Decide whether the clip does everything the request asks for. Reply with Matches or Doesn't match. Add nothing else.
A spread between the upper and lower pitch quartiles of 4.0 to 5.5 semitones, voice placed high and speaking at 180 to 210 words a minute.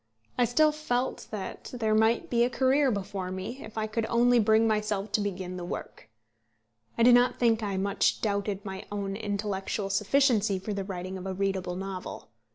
Doesn't match